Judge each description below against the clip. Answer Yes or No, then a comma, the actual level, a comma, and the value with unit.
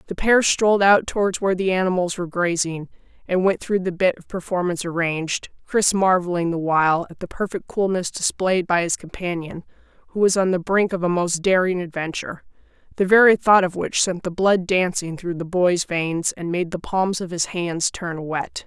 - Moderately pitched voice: Yes, medium, 180 Hz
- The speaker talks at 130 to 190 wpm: No, average, 200 wpm